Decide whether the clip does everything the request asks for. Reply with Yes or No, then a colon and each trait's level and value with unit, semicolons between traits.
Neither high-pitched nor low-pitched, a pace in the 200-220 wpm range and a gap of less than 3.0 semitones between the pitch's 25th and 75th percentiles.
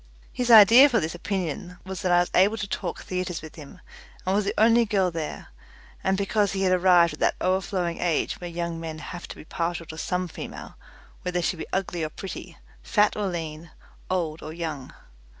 Yes: medium, 180 Hz; fast, 205 wpm; narrow, 2.6 semitones